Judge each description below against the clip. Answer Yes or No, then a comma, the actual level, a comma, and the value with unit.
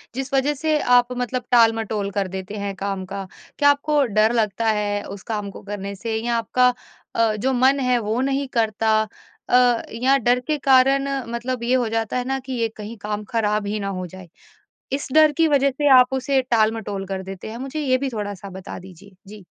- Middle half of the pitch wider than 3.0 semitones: Yes, average, 4.1 semitones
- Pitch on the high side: Yes, high, 230 Hz